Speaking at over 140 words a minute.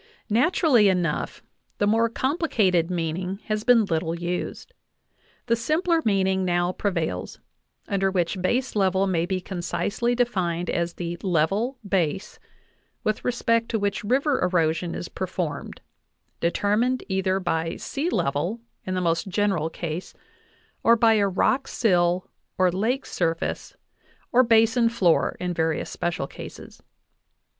No: slow, 135 wpm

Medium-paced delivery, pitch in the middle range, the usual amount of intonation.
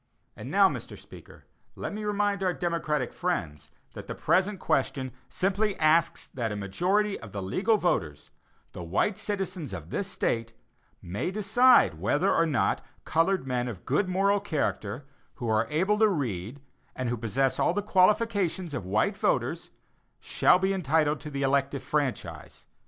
No: average, 160 wpm; medium, 160 Hz; wide, 8.1 semitones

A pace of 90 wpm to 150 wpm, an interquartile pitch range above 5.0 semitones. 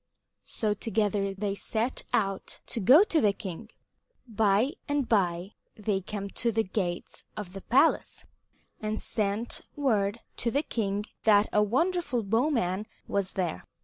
No: average, 145 wpm; average, 2.9 semitones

